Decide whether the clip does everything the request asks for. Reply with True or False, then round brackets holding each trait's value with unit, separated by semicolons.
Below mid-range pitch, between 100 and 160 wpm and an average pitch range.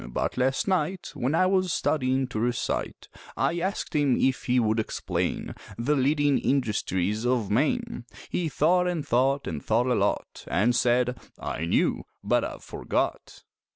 True (130 Hz; 155 wpm; 4.6 semitones)